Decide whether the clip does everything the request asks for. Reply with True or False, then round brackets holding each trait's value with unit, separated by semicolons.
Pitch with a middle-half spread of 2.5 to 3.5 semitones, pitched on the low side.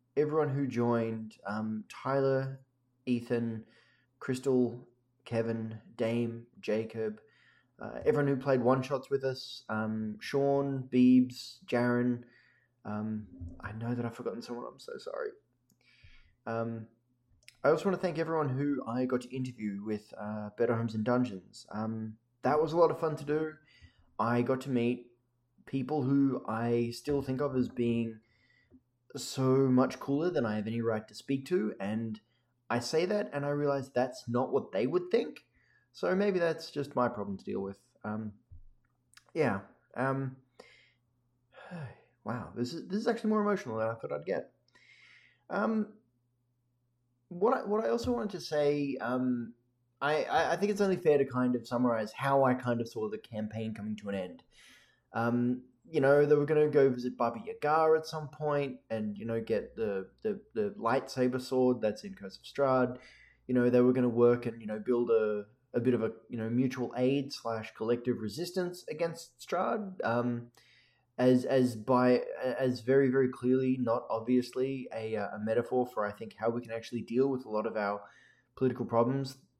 True (3.1 semitones; 125 Hz)